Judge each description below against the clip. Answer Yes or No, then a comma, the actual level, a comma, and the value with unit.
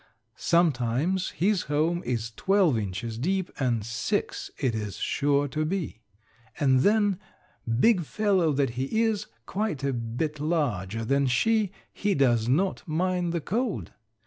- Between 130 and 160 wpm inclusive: Yes, average, 140 wpm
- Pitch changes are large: Yes, wide, 7.4 semitones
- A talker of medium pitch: Yes, medium, 150 Hz